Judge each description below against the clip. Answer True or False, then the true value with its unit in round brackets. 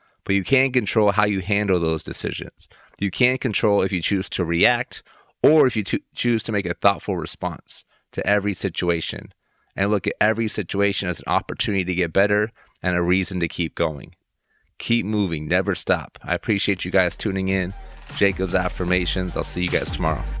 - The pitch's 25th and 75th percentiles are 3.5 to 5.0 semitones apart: False (2.5 semitones)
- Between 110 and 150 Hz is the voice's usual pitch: False (95 Hz)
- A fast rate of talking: False (190 wpm)